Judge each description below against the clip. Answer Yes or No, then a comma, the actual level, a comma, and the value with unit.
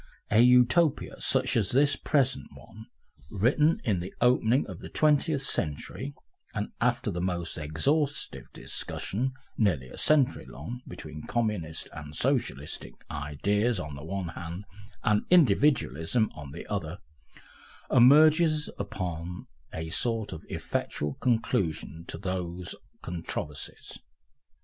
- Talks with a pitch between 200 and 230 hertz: No, low, 105 Hz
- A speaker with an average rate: No, slow, 120 wpm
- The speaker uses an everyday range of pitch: No, wide, 7.9 semitones